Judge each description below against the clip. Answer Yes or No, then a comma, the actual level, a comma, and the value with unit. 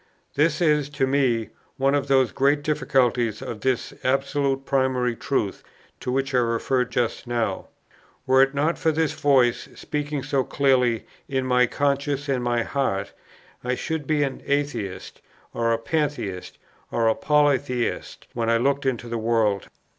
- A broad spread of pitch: No, average, 3.0 semitones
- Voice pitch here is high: No, low, 130 Hz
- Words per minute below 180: Yes, average, 155 wpm